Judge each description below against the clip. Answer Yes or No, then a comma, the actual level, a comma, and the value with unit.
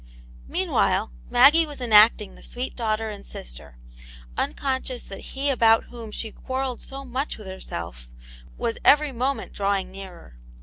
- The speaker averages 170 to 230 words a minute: No, average, 145 wpm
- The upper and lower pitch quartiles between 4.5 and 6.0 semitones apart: Yes, average, 5.1 semitones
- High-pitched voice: Yes, high, 230 Hz